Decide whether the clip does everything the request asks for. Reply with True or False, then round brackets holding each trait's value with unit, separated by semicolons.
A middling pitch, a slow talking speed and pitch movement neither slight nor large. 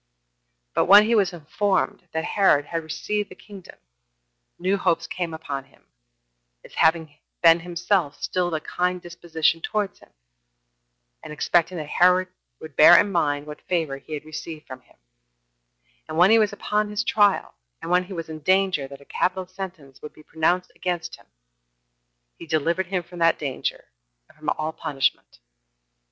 False (170 Hz; 170 wpm; 3.2 semitones)